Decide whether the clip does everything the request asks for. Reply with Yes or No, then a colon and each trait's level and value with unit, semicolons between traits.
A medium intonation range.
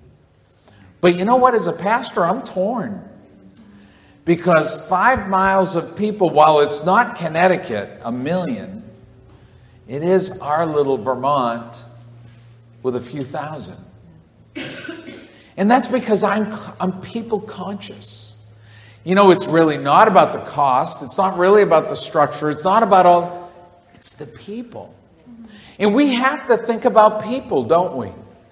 No: wide, 7.9 semitones